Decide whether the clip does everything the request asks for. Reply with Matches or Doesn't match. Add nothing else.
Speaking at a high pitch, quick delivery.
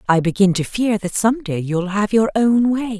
Matches